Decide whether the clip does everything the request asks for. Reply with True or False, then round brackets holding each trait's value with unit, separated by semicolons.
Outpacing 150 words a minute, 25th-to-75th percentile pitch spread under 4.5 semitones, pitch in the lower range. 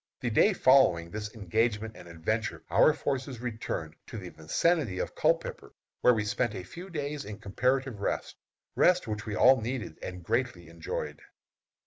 False (160 wpm; 4.8 semitones; 110 Hz)